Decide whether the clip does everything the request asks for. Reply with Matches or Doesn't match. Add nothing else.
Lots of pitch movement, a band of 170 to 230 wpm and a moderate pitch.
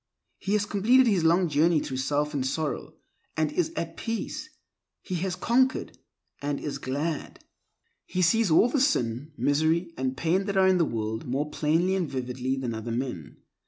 Matches